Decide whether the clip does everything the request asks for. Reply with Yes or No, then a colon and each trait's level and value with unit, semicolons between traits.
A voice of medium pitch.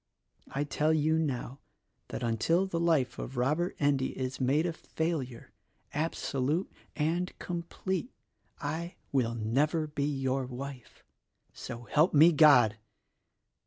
Yes: medium, 145 Hz